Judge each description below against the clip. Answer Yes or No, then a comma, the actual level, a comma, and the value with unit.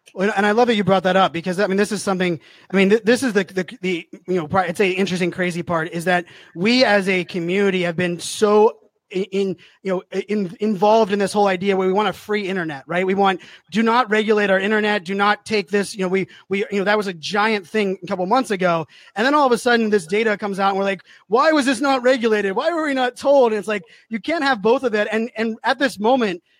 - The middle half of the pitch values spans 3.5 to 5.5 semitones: No, average, 2.8 semitones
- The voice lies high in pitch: Yes, high, 205 Hz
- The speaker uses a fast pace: Yes, fast, 260 wpm